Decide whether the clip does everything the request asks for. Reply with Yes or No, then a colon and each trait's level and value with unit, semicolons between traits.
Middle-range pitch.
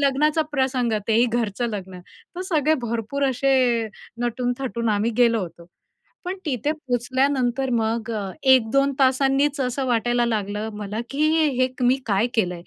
No: high, 245 Hz